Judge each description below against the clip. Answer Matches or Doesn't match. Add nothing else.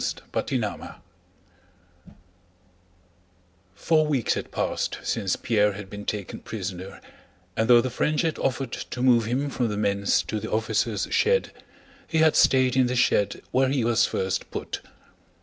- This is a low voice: Matches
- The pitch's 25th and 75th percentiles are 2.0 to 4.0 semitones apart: Doesn't match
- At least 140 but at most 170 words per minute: Matches